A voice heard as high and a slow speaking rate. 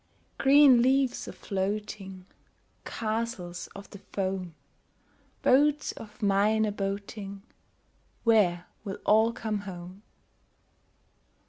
Yes: high, 205 Hz; slow, 95 wpm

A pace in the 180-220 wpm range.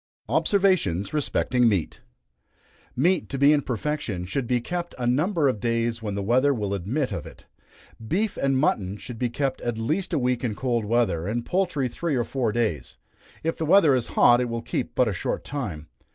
Yes: average, 195 wpm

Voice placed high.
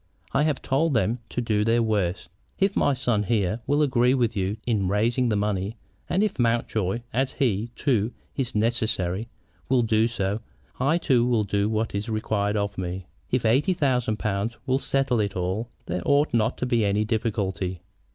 No: low, 115 Hz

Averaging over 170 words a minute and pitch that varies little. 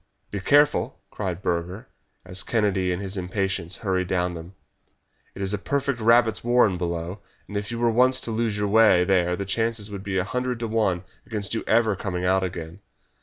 No: average, 195 wpm; average, 3.7 semitones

